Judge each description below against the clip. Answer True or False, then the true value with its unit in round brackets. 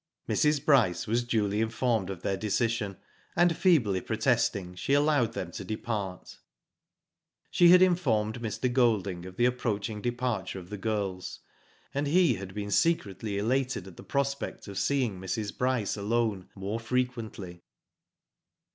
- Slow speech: False (145 wpm)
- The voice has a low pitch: True (110 Hz)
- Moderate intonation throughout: True (4.4 semitones)